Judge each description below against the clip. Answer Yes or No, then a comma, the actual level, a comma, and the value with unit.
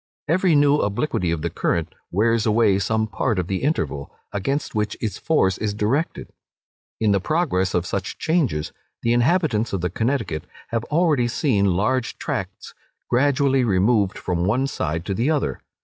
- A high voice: No, low, 110 Hz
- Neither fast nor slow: Yes, average, 165 wpm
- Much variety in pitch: Yes, wide, 6.3 semitones